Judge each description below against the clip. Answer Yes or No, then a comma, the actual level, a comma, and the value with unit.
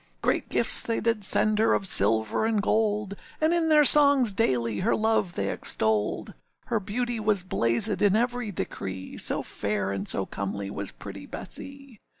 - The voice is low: No, high, 205 Hz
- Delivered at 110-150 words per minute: No, average, 165 wpm